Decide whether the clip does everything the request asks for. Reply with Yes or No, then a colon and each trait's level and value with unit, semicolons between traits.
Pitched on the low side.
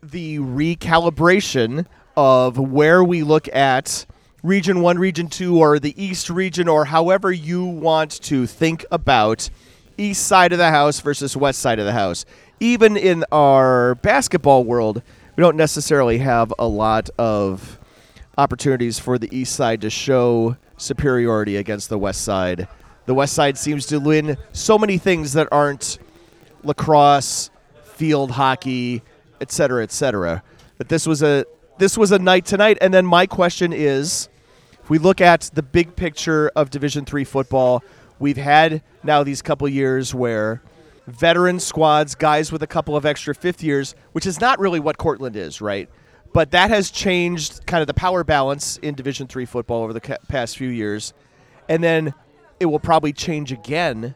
No: medium, 150 Hz